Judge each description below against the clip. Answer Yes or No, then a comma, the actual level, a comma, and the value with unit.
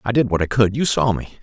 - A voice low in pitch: Yes, low, 110 Hz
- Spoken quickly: Yes, fast, 335 wpm